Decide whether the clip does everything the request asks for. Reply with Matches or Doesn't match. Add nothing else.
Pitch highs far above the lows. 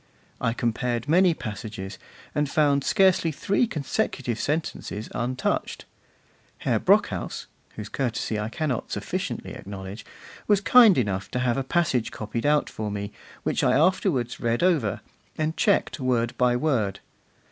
Matches